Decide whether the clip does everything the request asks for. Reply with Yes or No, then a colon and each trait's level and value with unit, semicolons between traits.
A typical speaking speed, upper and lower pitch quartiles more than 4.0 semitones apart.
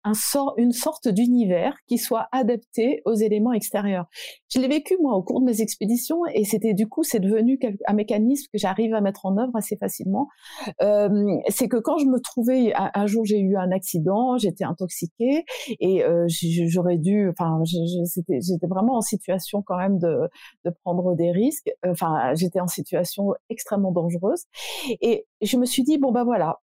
Yes: average, 180 wpm; average, 5.1 semitones